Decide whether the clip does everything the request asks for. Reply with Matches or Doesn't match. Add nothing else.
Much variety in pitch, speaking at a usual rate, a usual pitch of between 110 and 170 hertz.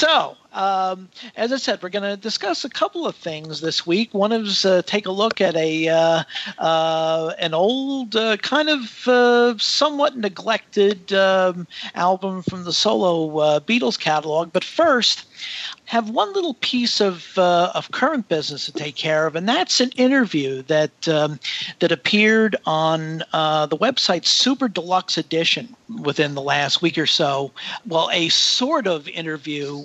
Doesn't match